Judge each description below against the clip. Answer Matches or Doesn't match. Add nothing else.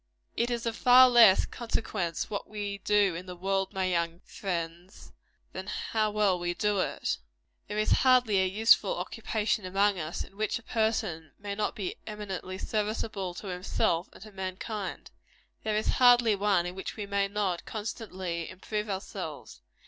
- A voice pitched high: Matches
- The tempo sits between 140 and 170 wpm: Matches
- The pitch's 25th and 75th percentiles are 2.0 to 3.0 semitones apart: Matches